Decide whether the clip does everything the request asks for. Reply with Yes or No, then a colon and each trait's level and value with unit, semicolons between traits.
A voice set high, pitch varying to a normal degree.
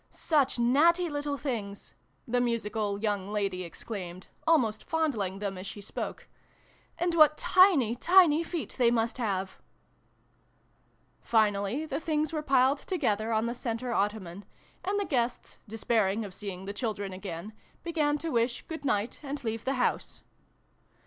No: high, 235 Hz; wide, 6.4 semitones